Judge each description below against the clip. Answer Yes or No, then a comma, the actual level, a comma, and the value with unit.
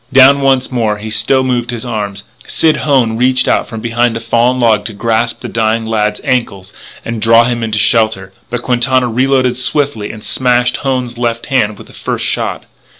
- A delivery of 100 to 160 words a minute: No, average, 190 wpm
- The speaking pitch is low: Yes, low, 120 Hz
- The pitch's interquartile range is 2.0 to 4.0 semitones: Yes, narrow, 2.4 semitones